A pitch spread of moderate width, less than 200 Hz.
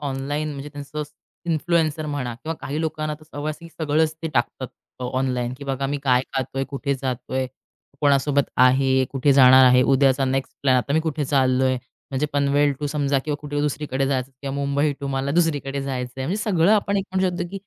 No: narrow, 2.3 semitones; medium, 140 Hz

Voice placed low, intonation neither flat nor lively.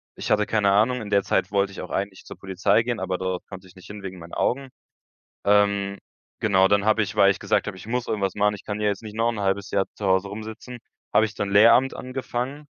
No: low, 100 Hz; narrow, 2.2 semitones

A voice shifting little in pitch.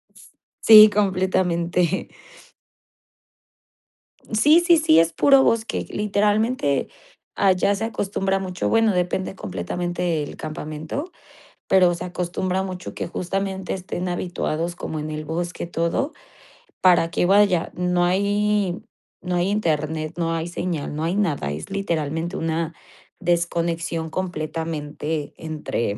No: average, 3.1 semitones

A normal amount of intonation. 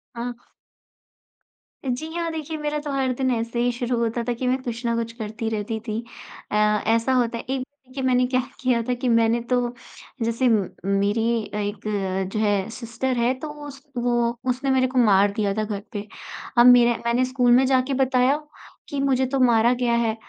No: narrow, 2.3 semitones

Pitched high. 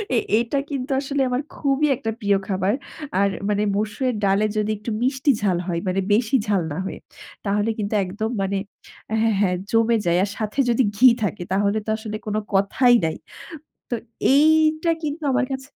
Yes: high, 220 Hz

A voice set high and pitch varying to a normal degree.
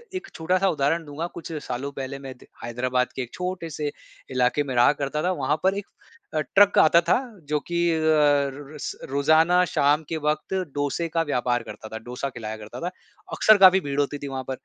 No: medium, 145 Hz; average, 4.1 semitones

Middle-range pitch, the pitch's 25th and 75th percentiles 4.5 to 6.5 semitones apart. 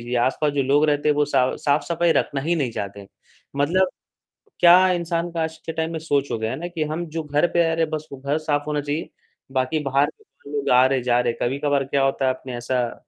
No: medium, 145 Hz; average, 3.5 semitones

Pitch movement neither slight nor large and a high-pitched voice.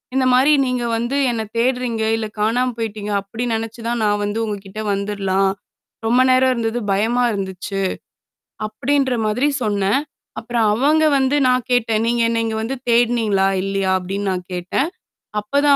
Yes: average, 3.5 semitones; high, 225 Hz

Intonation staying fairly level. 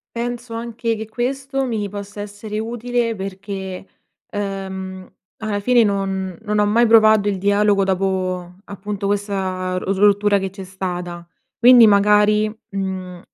Yes: narrow, 2.3 semitones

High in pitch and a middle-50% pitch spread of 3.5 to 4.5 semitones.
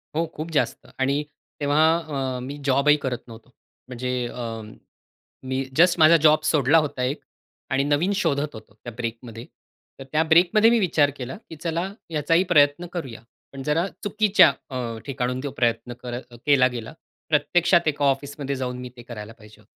No: medium, 140 Hz; average, 4.1 semitones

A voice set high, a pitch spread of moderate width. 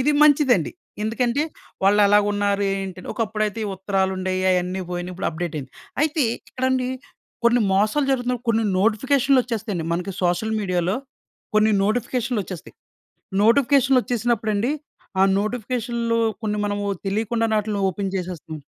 Yes: high, 215 Hz; average, 4.2 semitones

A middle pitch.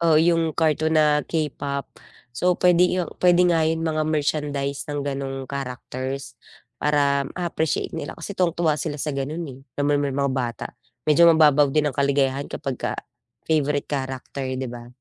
Yes: medium, 145 Hz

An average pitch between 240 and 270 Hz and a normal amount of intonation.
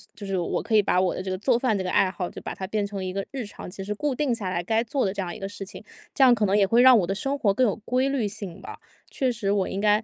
No: high, 205 Hz; average, 3.9 semitones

